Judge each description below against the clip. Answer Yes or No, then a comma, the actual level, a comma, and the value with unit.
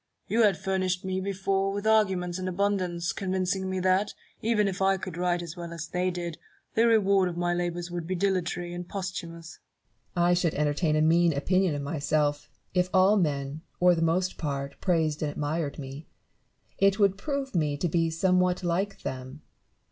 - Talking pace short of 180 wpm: No, average, 185 wpm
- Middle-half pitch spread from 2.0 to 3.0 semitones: Yes, narrow, 2.6 semitones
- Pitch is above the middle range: No, medium, 180 Hz